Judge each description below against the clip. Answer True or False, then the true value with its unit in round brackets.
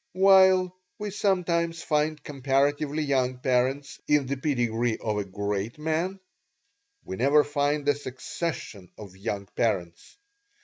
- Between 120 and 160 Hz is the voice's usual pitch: True (140 Hz)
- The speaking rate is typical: False (125 wpm)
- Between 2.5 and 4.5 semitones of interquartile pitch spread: False (5.3 semitones)